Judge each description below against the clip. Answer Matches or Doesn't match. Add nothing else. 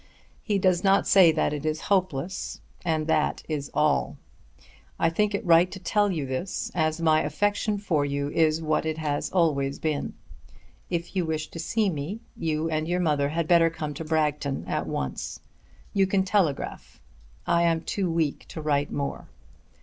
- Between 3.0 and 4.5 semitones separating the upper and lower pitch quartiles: Matches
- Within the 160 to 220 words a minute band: Matches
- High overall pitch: Doesn't match